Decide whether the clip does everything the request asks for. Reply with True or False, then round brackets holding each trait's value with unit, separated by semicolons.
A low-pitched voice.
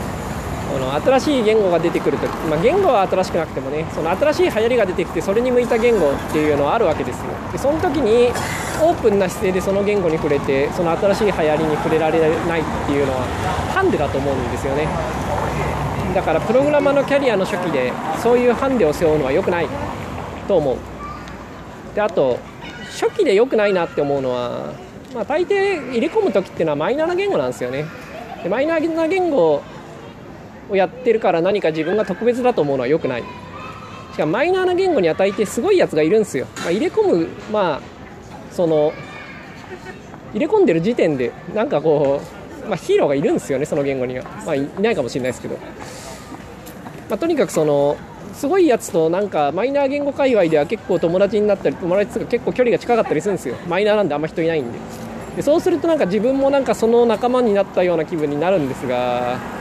False (205 Hz)